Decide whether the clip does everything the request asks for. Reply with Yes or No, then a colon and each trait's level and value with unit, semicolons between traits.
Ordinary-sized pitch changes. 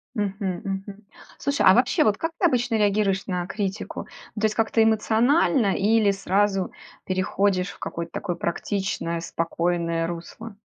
Yes: average, 3.1 semitones